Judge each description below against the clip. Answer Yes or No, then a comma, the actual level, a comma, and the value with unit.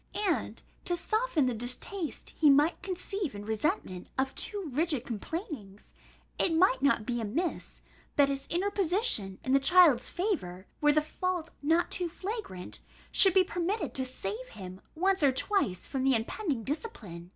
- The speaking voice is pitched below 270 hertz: No, very high, 300 Hz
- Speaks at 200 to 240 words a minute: No, average, 155 wpm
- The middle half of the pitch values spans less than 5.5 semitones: No, wide, 7.5 semitones